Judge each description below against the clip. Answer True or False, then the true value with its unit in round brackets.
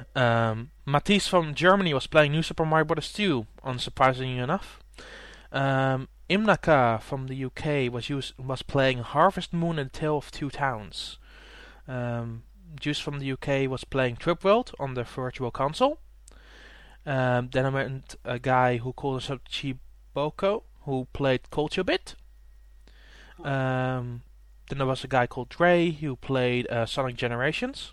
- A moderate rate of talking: True (150 wpm)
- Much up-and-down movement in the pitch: False (3.4 semitones)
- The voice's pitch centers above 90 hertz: True (135 Hz)